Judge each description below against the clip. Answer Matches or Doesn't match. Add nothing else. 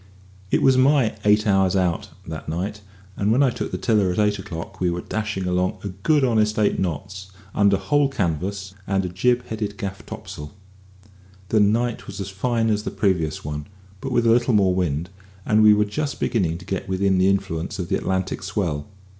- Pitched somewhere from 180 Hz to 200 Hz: Doesn't match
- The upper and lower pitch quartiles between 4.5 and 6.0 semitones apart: Doesn't match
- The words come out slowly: Doesn't match